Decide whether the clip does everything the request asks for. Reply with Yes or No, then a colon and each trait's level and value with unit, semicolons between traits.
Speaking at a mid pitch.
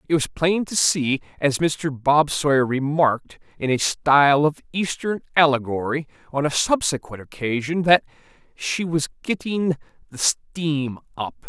Yes: medium, 150 Hz